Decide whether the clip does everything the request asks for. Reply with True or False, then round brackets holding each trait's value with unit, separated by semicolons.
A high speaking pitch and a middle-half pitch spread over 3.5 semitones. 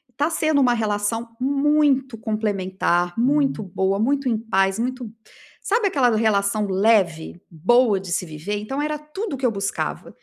True (225 Hz; 5.6 semitones)